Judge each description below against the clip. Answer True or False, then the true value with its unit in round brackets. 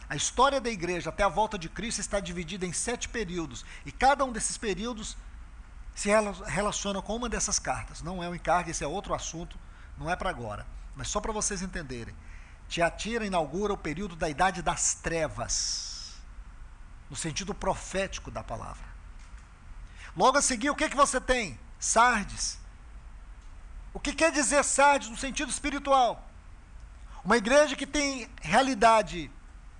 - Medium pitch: True (180 Hz)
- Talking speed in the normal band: True (155 wpm)